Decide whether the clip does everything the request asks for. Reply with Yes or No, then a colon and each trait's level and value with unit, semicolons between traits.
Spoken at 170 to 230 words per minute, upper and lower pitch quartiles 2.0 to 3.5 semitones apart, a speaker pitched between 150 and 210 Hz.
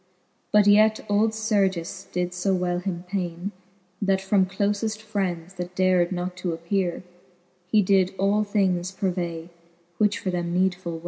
No: average, 145 wpm; narrow, 2.4 semitones; medium, 185 Hz